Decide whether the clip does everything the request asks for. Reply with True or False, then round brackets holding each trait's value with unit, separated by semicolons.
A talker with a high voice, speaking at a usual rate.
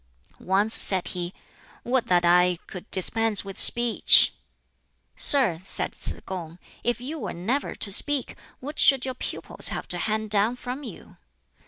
True (215 Hz; 155 wpm)